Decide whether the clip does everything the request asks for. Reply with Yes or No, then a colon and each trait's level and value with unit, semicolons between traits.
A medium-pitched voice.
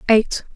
No: high, 220 Hz